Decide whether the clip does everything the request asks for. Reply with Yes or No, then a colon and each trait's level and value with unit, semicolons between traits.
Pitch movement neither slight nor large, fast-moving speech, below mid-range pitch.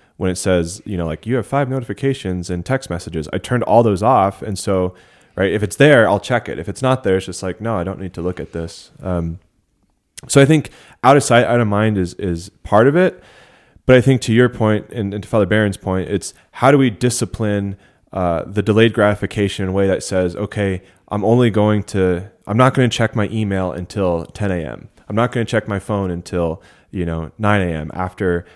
Yes: average, 3.9 semitones; fast, 235 wpm; low, 100 Hz